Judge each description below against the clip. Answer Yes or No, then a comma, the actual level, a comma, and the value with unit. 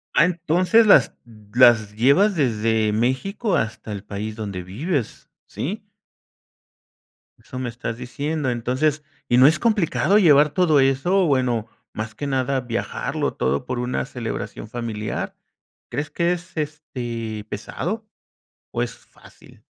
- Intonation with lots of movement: Yes, wide, 6.2 semitones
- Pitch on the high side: No, low, 130 Hz